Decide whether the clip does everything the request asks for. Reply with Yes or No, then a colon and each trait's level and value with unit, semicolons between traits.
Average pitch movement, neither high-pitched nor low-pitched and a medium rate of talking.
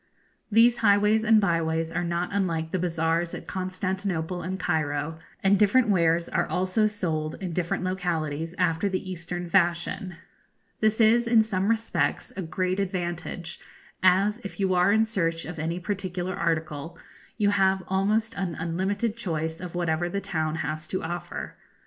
Yes: average, 3.2 semitones; medium, 180 Hz; average, 155 wpm